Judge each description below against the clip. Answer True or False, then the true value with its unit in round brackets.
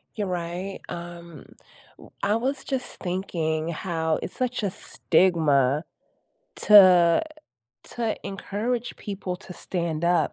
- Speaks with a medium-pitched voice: True (180 Hz)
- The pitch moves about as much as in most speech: True (3.6 semitones)